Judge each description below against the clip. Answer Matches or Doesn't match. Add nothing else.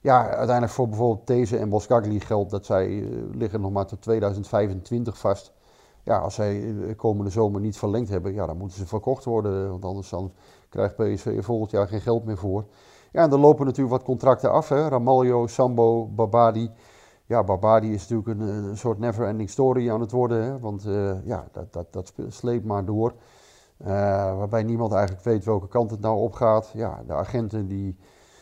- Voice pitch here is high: Doesn't match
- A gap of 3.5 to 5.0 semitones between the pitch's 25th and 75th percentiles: Doesn't match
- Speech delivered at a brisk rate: Doesn't match